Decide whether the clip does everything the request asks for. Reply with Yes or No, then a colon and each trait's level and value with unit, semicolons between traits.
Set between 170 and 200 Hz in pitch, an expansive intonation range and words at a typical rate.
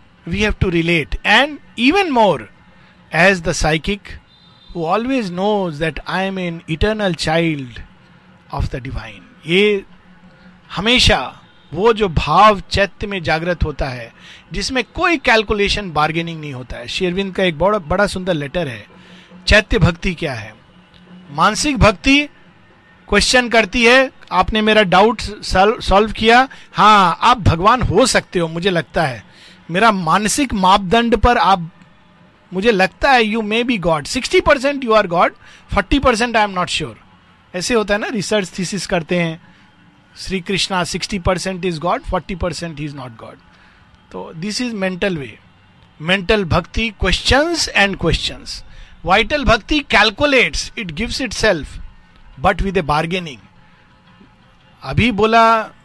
No: high, 190 Hz; average, 4.7 semitones; average, 140 wpm